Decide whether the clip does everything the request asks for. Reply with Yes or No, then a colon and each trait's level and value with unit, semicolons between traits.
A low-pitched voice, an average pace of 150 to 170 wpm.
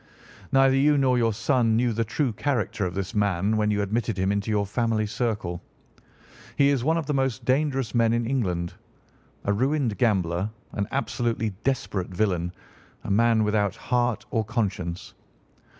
Yes: low, 115 Hz; average, 160 wpm